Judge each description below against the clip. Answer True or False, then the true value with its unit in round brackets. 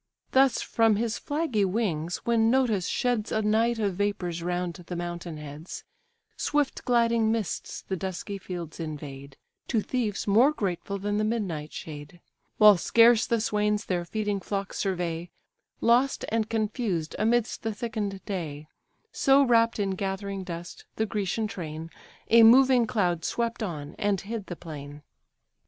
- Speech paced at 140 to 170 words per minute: True (145 wpm)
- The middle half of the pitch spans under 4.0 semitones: False (4.7 semitones)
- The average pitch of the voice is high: True (205 Hz)